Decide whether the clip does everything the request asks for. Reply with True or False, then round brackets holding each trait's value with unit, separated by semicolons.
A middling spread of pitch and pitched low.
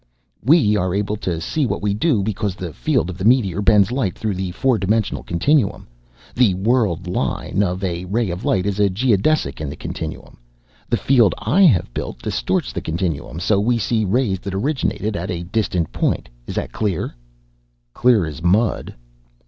True (4.0 semitones; 100 Hz)